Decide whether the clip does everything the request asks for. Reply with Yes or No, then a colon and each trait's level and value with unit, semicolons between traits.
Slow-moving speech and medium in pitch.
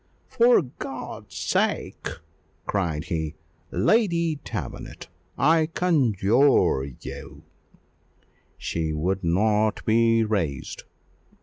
No: slow, 85 wpm; low, 110 Hz